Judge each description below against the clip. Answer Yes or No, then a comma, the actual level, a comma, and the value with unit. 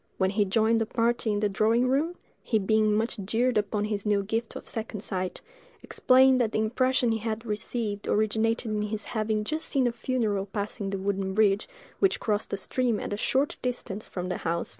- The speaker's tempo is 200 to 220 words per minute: Yes, fast, 205 wpm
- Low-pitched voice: No, high, 215 Hz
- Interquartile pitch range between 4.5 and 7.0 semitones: No, narrow, 2.4 semitones